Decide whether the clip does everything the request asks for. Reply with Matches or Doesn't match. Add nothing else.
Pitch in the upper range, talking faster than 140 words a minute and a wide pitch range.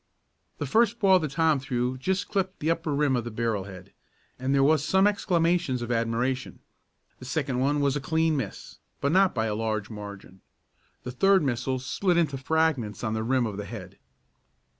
Doesn't match